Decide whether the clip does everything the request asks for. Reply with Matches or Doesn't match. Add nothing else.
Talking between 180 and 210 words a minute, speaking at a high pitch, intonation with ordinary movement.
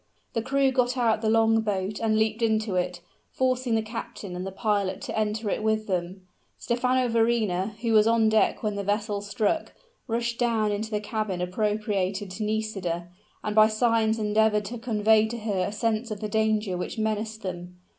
Doesn't match